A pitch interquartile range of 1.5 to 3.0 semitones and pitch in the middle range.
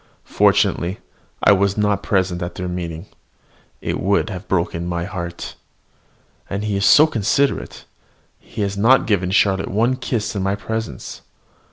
No: average, 2.7 semitones; low, 100 Hz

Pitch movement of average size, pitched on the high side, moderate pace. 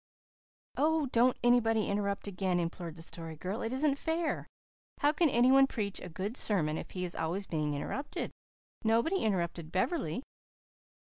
No: wide, 6.9 semitones; high, 205 Hz; average, 155 wpm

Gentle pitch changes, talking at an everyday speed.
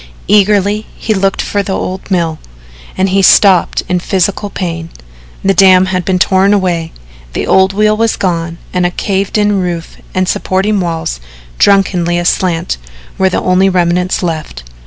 Yes: narrow, 2.2 semitones; average, 155 wpm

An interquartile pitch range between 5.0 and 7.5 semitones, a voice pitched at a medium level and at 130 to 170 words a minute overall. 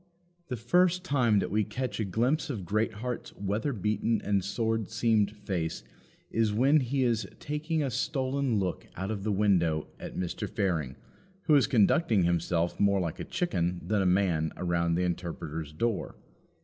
No: wide, 5.4 semitones; low, 105 Hz; average, 165 wpm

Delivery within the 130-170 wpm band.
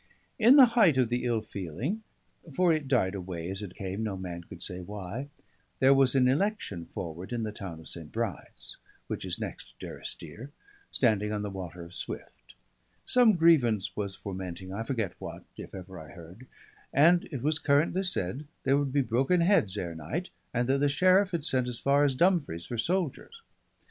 No: average, 195 wpm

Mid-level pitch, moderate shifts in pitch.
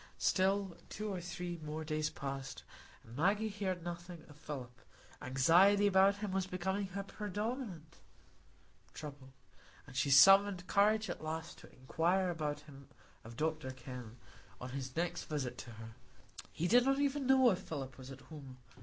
No: medium, 165 Hz; wide, 6.2 semitones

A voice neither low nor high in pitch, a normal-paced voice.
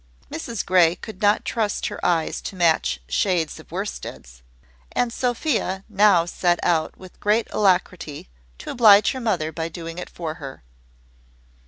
Yes: medium, 180 Hz; average, 150 wpm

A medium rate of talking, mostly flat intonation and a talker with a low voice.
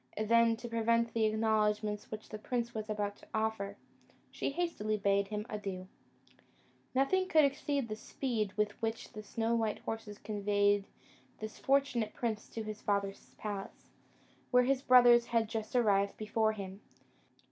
No: average, 150 wpm; narrow, 2.0 semitones; high, 220 Hz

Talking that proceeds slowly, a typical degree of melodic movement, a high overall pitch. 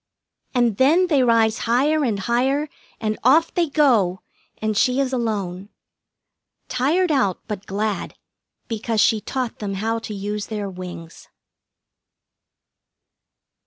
Yes: slow, 125 wpm; average, 4.4 semitones; high, 225 Hz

